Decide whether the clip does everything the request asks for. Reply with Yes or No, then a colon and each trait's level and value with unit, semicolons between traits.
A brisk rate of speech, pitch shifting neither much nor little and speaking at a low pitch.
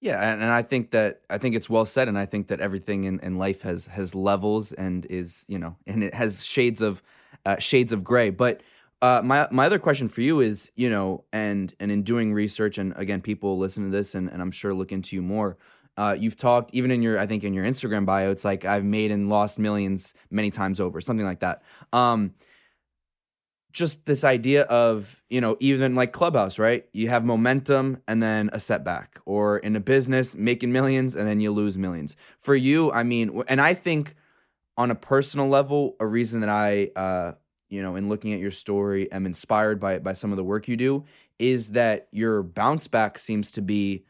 Yes: fast, 215 wpm; average, 3.7 semitones; low, 105 Hz